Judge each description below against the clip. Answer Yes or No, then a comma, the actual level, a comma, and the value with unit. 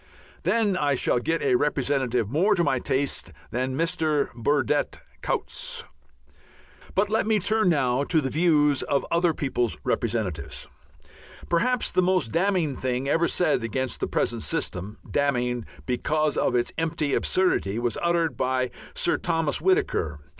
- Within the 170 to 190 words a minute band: No, average, 145 wpm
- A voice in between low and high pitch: Yes, medium, 145 Hz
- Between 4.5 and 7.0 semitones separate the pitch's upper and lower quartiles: Yes, wide, 5.5 semitones